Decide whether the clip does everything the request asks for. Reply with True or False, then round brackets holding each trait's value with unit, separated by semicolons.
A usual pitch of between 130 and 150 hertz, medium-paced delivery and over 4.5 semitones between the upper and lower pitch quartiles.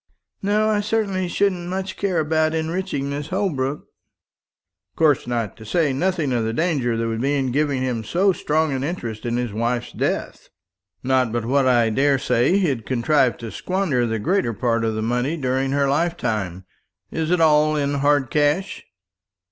True (140 Hz; 175 wpm; 5.6 semitones)